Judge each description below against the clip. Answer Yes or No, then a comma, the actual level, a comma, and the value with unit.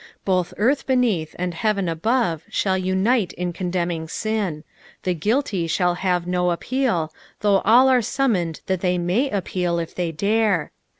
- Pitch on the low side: No, medium, 185 Hz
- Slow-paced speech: No, average, 155 wpm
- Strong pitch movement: No, average, 4.0 semitones